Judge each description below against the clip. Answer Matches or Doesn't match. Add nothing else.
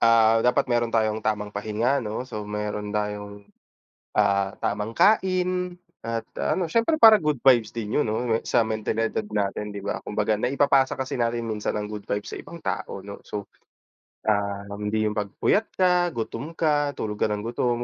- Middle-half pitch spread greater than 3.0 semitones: Matches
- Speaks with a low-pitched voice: Matches